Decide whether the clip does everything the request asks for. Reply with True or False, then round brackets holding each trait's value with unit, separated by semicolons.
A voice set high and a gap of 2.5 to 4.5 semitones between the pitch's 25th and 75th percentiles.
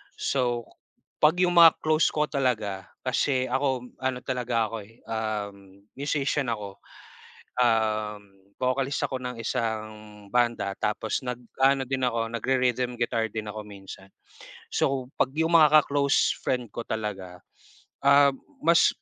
False (125 Hz; 3.8 semitones)